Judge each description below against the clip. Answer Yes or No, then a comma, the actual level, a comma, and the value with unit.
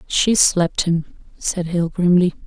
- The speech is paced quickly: No, average, 145 wpm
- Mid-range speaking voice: Yes, medium, 175 Hz